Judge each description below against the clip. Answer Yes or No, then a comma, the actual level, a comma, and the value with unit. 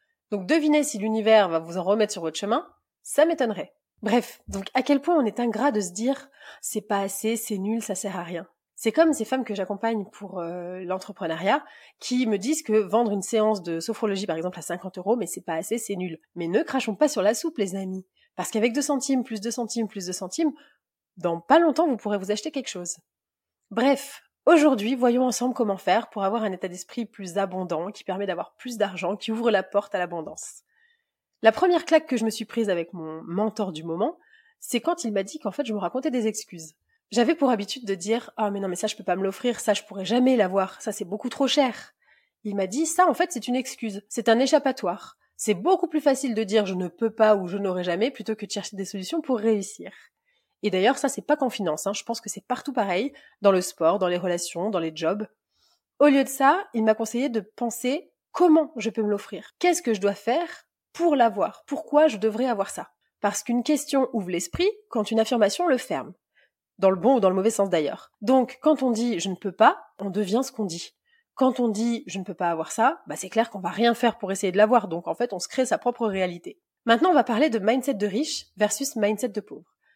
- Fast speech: Yes, fast, 240 wpm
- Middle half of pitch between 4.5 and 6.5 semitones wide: Yes, average, 4.9 semitones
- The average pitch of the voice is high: Yes, high, 220 Hz